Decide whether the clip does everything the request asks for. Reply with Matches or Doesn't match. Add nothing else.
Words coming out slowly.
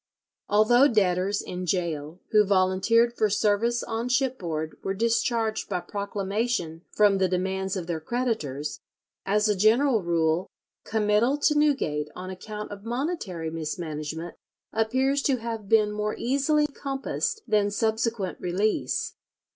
Matches